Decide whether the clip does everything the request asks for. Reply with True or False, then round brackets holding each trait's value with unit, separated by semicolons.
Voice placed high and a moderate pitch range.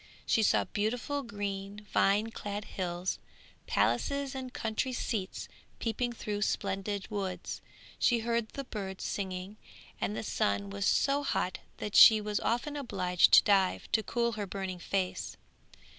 True (210 Hz; 3.4 semitones)